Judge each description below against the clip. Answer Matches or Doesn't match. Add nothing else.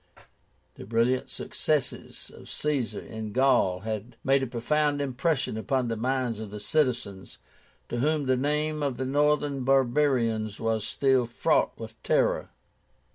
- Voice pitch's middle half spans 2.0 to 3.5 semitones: Doesn't match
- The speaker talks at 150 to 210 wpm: Doesn't match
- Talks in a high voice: Doesn't match